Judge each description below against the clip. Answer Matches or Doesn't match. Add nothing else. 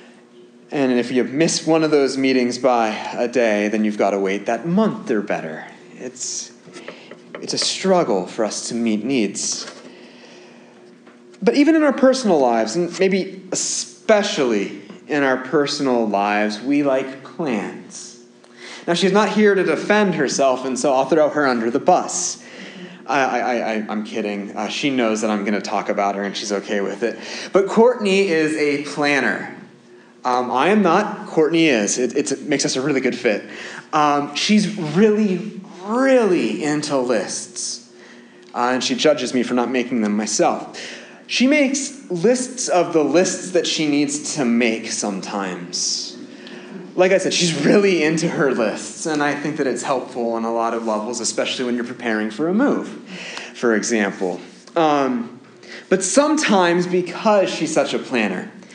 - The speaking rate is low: Doesn't match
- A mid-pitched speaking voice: Matches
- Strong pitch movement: Matches